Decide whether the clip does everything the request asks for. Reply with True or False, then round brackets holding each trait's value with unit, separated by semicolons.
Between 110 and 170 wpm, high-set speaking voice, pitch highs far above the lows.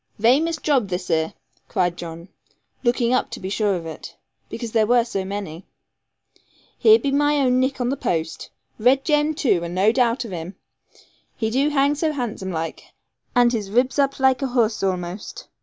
False (185 wpm; 235 Hz; 6.2 semitones)